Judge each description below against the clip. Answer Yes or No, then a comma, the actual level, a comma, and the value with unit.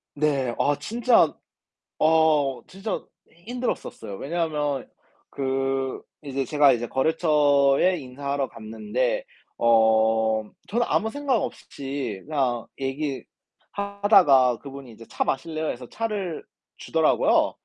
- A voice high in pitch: No, medium, 140 Hz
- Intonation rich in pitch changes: No, average, 4.9 semitones